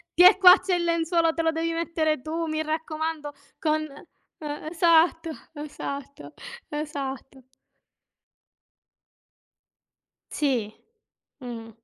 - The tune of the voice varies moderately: No, narrow, 2.3 semitones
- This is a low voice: No, very high, 315 Hz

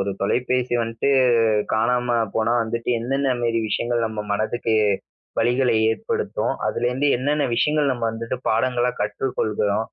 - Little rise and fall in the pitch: Yes, narrow, 2.3 semitones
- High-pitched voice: No, low, 120 Hz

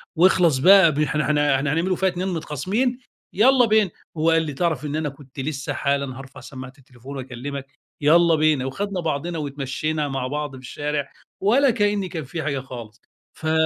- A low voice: No, medium, 150 Hz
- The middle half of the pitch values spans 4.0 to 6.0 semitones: Yes, average, 4.3 semitones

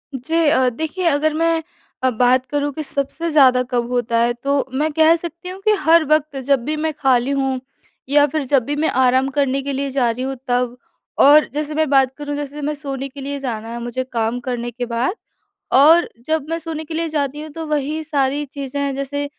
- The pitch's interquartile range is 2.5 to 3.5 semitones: Yes, average, 3.1 semitones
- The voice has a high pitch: Yes, very high, 280 Hz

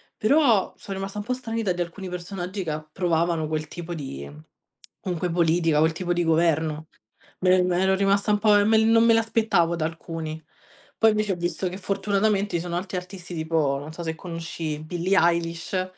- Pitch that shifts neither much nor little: Yes, average, 3.3 semitones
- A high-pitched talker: No, medium, 175 Hz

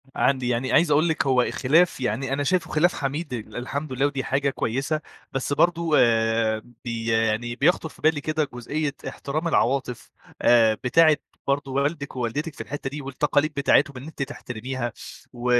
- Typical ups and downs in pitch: Yes, average, 3.6 semitones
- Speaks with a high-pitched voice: No, low, 135 Hz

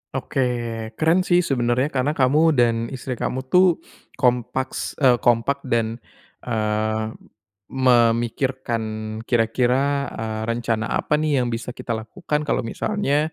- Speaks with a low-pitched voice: Yes, low, 125 Hz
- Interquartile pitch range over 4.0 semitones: No, average, 3.4 semitones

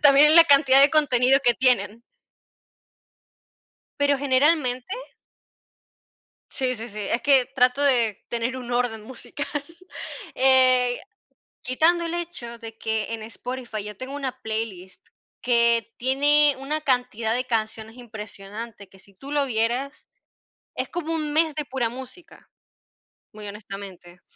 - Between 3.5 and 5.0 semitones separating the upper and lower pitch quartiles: Yes, average, 3.8 semitones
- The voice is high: Yes, very high, 250 Hz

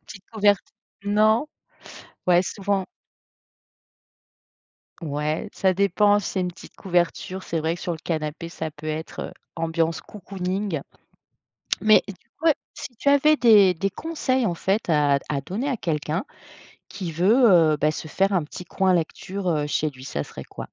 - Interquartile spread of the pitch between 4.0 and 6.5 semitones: Yes, average, 4.3 semitones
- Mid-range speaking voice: Yes, medium, 180 Hz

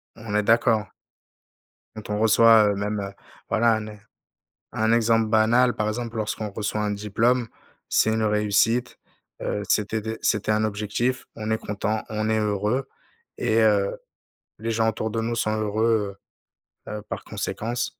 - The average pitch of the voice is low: Yes, low, 110 Hz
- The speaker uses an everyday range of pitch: No, narrow, 1.4 semitones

